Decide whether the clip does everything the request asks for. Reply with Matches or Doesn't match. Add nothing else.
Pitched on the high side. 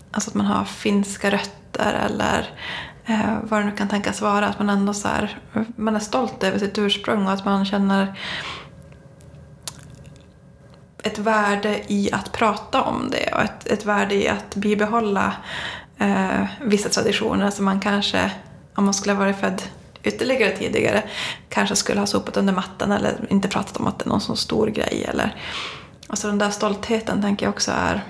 Matches